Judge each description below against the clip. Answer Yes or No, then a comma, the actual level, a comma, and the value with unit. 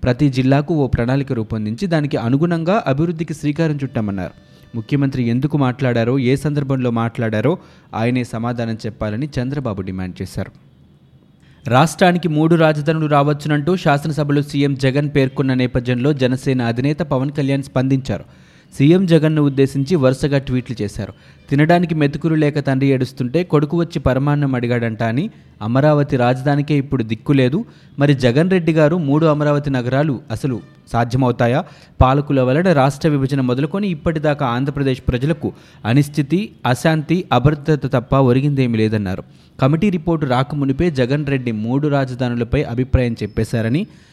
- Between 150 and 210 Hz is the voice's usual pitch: No, low, 135 Hz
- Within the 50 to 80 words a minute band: No, average, 120 wpm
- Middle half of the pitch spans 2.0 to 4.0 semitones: Yes, average, 3.4 semitones